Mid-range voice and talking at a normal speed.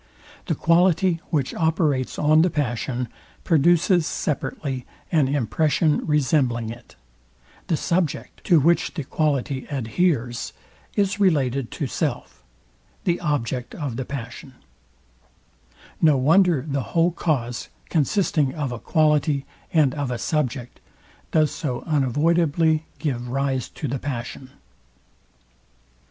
No: medium, 145 Hz; slow, 115 wpm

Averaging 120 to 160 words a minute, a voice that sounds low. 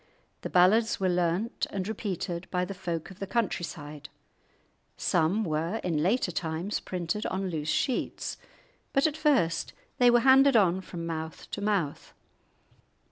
No: average, 150 wpm; medium, 185 Hz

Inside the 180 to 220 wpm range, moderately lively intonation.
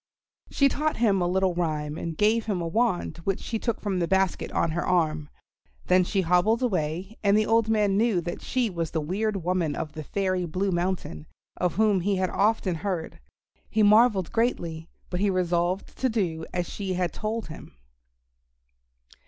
Yes: average, 185 wpm; average, 3.8 semitones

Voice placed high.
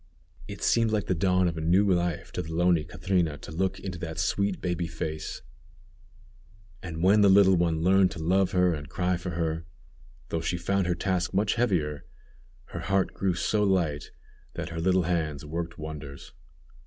No: very low, 90 Hz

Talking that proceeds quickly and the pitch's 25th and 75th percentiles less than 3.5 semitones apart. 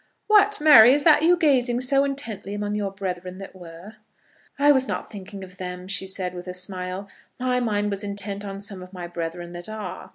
No: fast, 220 wpm; wide, 5.4 semitones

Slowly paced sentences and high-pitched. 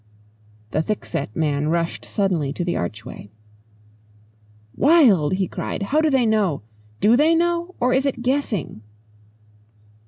Yes: slow, 130 wpm; high, 205 Hz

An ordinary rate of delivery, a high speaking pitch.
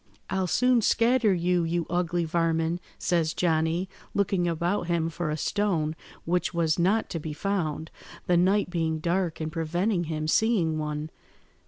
No: average, 155 wpm; medium, 170 Hz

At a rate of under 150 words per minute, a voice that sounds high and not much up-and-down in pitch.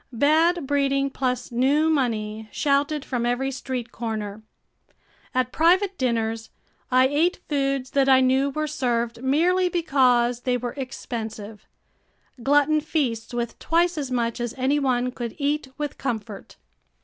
No: slow, 135 wpm; very high, 260 Hz; average, 3.4 semitones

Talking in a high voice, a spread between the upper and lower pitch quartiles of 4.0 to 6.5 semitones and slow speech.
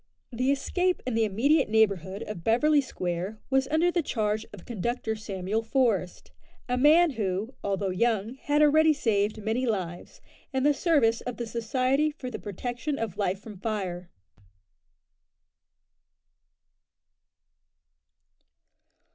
Yes: high, 225 Hz; average, 4.9 semitones; slow, 125 wpm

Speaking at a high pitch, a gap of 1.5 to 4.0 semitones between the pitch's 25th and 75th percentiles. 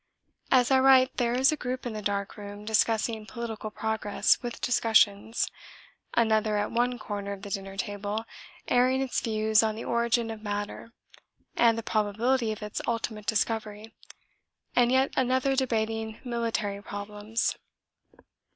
Yes: high, 225 Hz; narrow, 2.5 semitones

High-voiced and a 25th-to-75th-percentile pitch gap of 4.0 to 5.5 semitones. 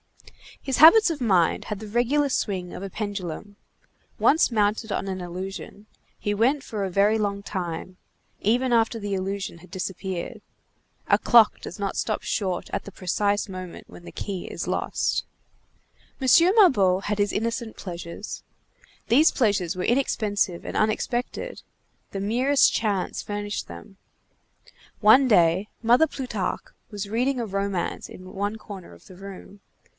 No: high, 205 Hz; average, 3.5 semitones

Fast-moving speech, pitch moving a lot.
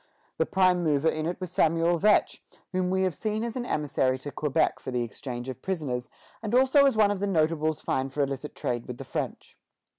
Yes: fast, 215 wpm; wide, 5.7 semitones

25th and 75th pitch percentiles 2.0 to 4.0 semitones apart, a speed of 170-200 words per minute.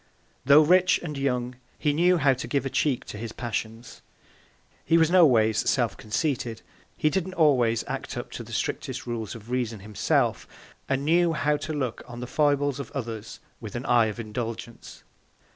No: average, 4.5 semitones; average, 180 wpm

